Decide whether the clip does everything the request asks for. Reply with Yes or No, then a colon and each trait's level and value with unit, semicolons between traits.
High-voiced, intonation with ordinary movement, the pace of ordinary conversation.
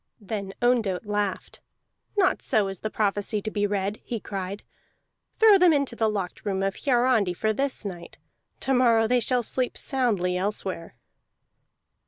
Yes: high, 215 Hz; average, 4.0 semitones; average, 155 wpm